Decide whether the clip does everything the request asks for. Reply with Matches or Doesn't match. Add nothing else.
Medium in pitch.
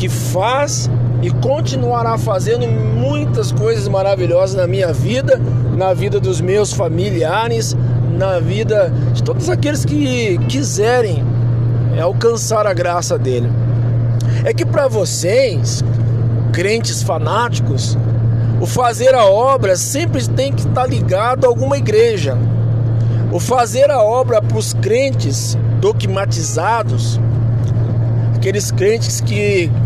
Doesn't match